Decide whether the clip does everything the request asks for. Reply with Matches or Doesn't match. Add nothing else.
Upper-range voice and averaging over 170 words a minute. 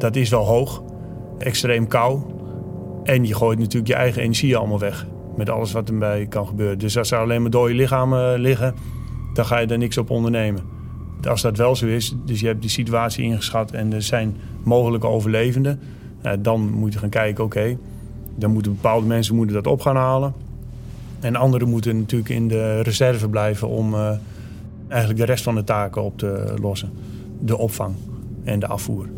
Doesn't match